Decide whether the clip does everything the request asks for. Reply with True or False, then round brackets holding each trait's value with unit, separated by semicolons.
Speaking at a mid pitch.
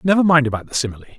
True (145 Hz)